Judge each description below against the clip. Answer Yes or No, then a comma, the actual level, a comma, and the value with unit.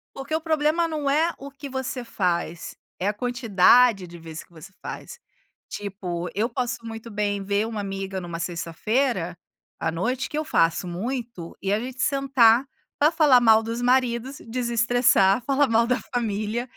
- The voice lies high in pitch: Yes, high, 230 Hz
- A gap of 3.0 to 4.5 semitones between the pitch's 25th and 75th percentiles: No, average, 5.2 semitones